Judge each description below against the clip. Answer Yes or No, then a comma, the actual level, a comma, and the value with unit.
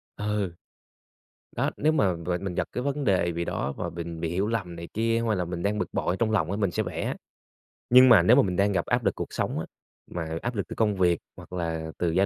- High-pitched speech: No, very low, 95 Hz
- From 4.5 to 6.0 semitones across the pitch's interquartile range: No, average, 3.8 semitones